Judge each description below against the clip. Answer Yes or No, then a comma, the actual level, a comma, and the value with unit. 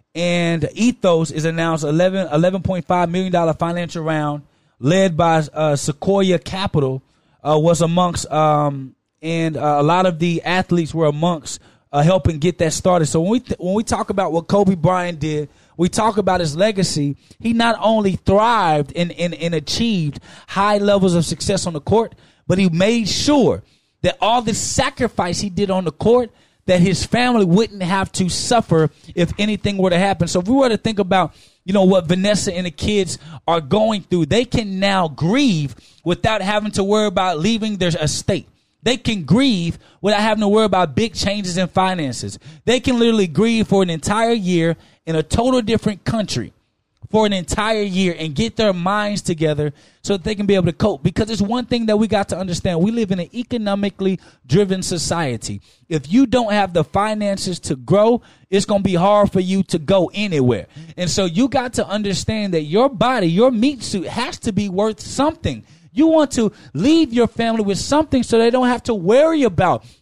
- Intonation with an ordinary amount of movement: Yes, average, 4.5 semitones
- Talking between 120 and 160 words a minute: No, average, 195 wpm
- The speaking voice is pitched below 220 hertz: Yes, high, 190 Hz